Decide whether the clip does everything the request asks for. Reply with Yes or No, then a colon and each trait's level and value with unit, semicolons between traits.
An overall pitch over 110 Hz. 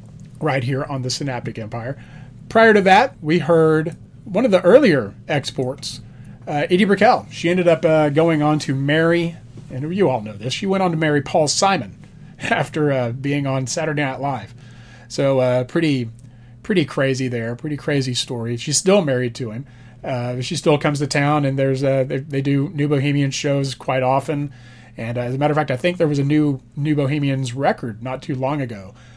Yes: medium, 140 Hz